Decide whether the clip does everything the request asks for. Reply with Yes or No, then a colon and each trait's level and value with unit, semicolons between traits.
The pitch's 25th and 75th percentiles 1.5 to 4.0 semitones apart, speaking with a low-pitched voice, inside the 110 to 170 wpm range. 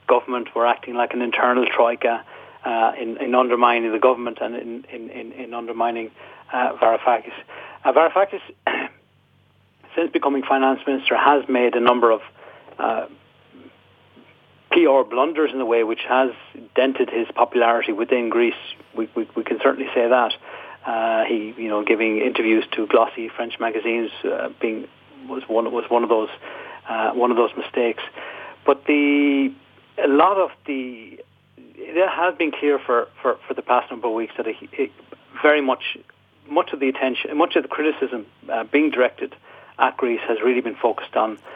Yes: average, 3.6 semitones; low, 125 Hz; average, 165 wpm